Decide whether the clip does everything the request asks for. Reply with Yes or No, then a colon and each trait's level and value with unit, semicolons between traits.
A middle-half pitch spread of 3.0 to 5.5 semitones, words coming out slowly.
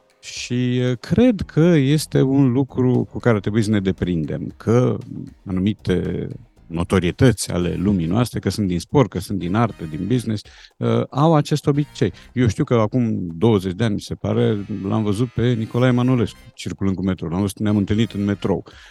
No: average, 4.5 semitones; fast, 170 wpm